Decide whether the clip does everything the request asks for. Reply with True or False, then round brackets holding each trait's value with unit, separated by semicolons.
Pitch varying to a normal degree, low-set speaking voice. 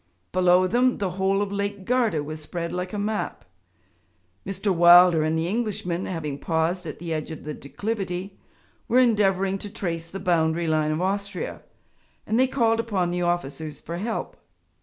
False (3.5 semitones; 180 Hz)